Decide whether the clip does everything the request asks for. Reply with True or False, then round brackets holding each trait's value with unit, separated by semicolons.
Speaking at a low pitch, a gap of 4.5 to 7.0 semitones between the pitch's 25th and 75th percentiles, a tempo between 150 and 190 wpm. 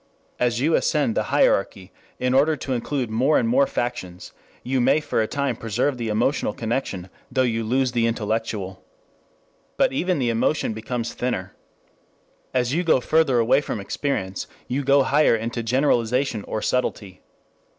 False (125 Hz; 3.7 semitones; 160 wpm)